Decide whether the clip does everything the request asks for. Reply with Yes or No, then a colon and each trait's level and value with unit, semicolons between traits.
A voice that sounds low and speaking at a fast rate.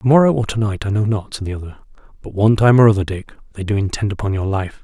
Yes: low, 105 Hz; fast, 285 wpm